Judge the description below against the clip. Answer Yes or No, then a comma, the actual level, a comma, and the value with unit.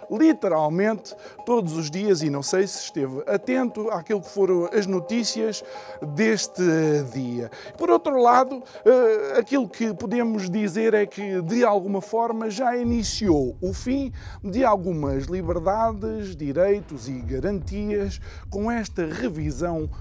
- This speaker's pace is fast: No, average, 125 wpm